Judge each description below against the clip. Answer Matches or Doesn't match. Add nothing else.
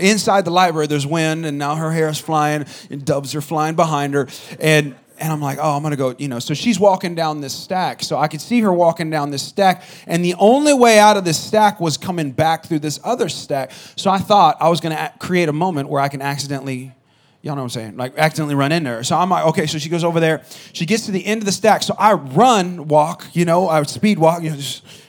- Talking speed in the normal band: Doesn't match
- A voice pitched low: Doesn't match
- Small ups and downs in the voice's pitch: Doesn't match